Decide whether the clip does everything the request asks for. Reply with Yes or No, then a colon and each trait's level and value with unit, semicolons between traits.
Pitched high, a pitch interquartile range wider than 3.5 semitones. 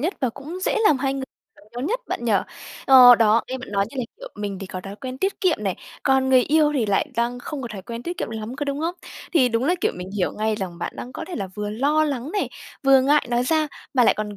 Yes: very high, 255 Hz; average, 5.2 semitones